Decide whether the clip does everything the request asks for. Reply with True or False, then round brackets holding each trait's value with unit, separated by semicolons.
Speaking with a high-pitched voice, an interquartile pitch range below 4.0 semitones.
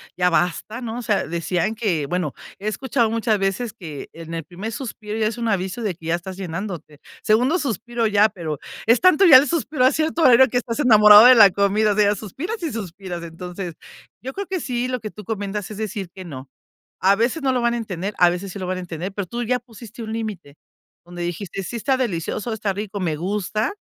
False (210 Hz; 4.8 semitones)